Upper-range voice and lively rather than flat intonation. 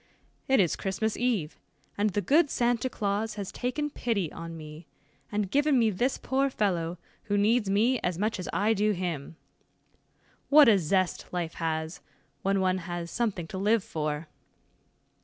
No: high, 200 Hz; average, 4.9 semitones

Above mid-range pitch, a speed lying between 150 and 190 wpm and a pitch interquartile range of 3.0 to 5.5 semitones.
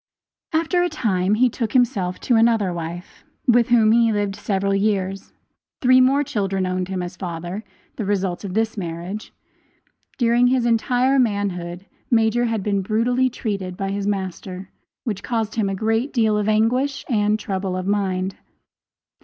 Yes: high, 210 Hz; average, 160 wpm; average, 3.7 semitones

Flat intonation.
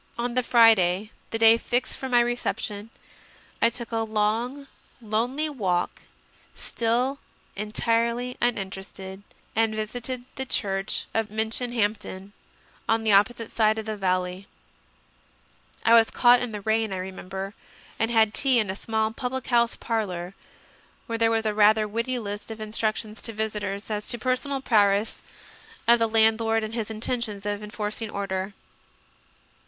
Yes: narrow, 2.3 semitones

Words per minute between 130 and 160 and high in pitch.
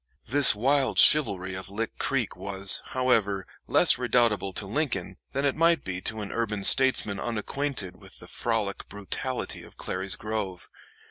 No: average, 150 wpm; low, 110 Hz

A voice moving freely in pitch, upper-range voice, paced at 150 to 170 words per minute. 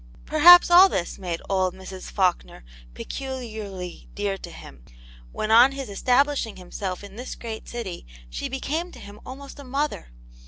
Yes: wide, 6.5 semitones; high, 220 Hz; average, 155 wpm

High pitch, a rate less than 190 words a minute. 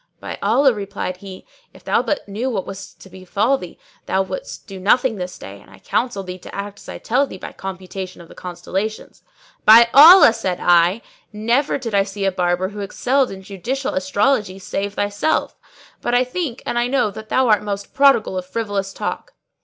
No: high, 205 Hz; average, 200 wpm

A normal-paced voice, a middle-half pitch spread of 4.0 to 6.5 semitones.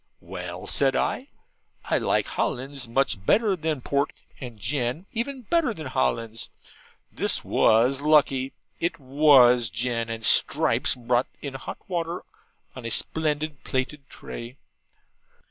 No: slow, 130 wpm; average, 4.5 semitones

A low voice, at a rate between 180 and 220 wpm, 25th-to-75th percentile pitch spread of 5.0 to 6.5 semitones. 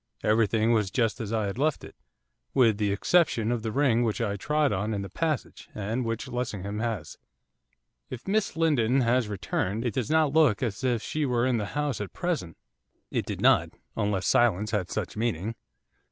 No: low, 115 Hz; average, 190 wpm; average, 3.8 semitones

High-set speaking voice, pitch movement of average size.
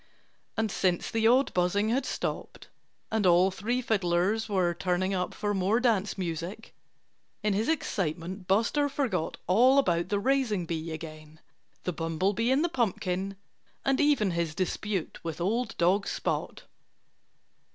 Yes: high, 195 Hz; average, 4.3 semitones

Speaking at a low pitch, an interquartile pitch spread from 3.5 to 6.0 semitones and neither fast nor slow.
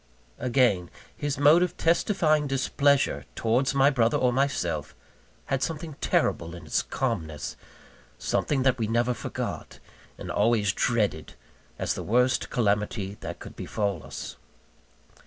No: low, 125 Hz; average, 5.0 semitones; slow, 130 wpm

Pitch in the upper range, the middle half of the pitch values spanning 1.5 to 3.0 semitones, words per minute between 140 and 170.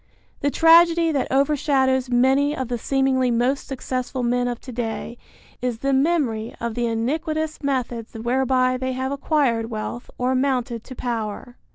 Yes: very high, 255 Hz; narrow, 2.5 semitones; average, 155 wpm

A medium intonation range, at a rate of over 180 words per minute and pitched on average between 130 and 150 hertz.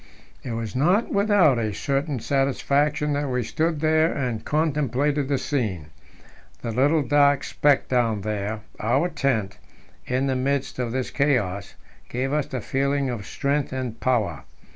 No: average, 3.8 semitones; average, 150 wpm; low, 135 Hz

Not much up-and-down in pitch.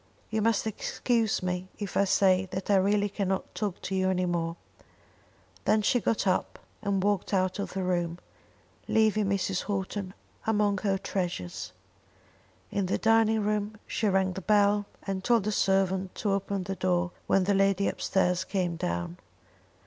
Yes: narrow, 1.9 semitones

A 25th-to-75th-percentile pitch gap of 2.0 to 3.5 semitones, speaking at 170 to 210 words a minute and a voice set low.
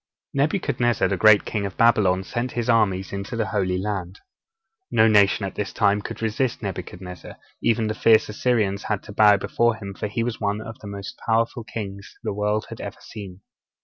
Yes: narrow, 2.5 semitones; average, 190 wpm; low, 105 Hz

